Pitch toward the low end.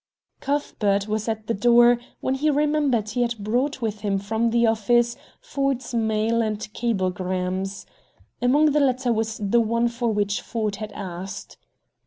No: high, 225 Hz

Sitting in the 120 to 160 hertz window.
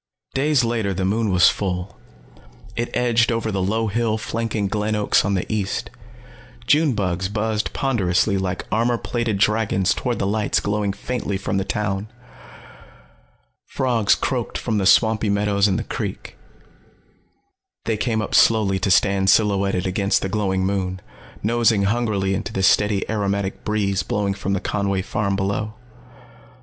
No: low, 105 Hz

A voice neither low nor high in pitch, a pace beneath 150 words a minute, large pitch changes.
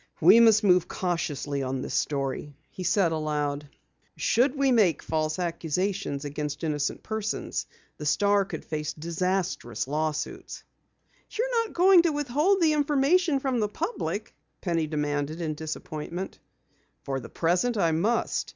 Yes: medium, 175 Hz; average, 140 wpm; wide, 7.9 semitones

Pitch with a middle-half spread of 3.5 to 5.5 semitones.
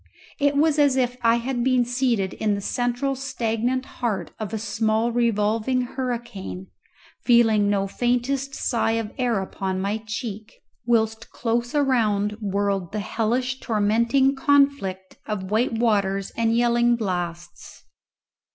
No: average, 3.1 semitones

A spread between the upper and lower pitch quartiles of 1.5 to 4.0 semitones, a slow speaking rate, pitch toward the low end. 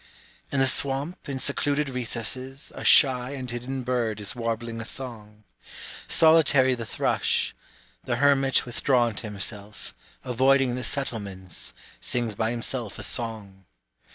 Yes: average, 3.1 semitones; slow, 130 wpm; low, 125 Hz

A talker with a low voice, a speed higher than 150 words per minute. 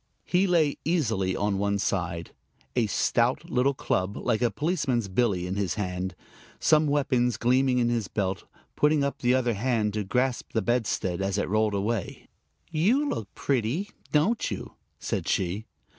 Yes: low, 120 Hz; average, 160 wpm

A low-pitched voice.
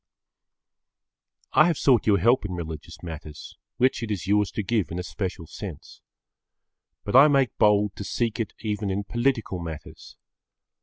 Yes: low, 105 Hz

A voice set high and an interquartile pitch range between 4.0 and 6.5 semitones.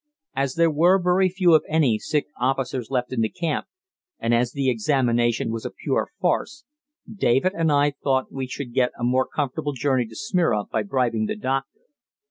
No: low, 135 Hz; average, 4.5 semitones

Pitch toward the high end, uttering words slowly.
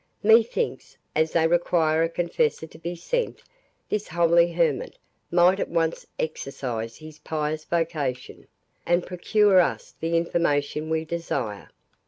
No: medium, 165 Hz; slow, 130 wpm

